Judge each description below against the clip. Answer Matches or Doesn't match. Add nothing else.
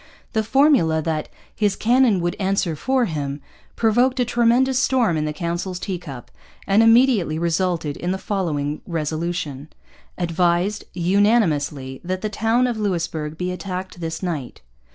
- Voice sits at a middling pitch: Matches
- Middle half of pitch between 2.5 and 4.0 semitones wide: Doesn't match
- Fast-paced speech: Doesn't match